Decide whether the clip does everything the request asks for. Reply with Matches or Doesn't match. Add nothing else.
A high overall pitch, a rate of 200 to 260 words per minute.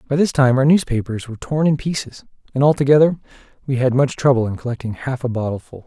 Doesn't match